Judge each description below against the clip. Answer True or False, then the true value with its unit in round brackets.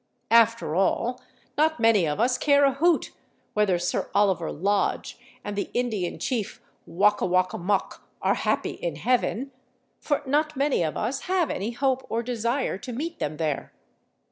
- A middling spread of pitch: False (5.9 semitones)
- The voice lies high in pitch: True (230 Hz)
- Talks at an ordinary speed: True (170 wpm)